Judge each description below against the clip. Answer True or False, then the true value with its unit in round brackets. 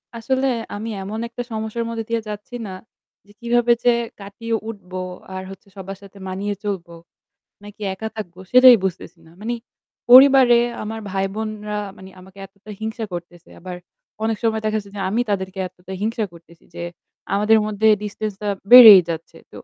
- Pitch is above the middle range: True (210 Hz)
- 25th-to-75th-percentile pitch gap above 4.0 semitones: False (2.9 semitones)